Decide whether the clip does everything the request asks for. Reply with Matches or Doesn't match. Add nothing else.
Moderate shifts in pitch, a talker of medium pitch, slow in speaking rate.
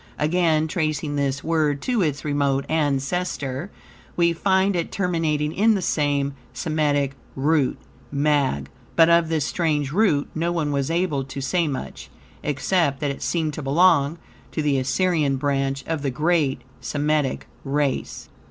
Doesn't match